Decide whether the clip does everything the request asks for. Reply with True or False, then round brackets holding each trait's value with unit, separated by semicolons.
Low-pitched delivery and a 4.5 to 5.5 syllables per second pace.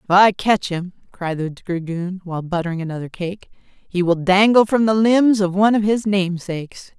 False (190 Hz; 5.0 syllables/s)